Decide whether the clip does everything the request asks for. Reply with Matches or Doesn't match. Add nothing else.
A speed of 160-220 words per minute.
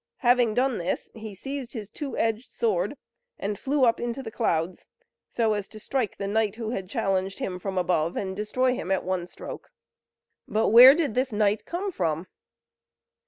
Matches